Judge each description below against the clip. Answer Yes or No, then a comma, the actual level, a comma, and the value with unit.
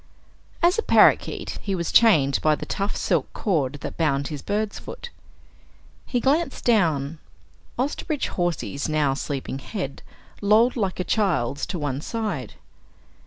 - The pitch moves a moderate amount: No, wide, 7.6 semitones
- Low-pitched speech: No, medium, 175 Hz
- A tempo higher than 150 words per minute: No, average, 140 wpm